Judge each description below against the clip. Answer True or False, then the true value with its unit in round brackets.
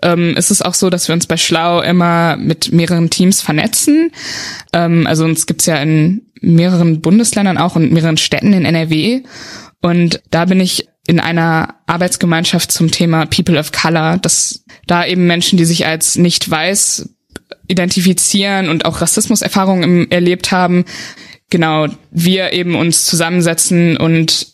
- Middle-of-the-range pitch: True (170 Hz)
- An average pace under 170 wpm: True (155 wpm)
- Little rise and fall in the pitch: True (2.1 semitones)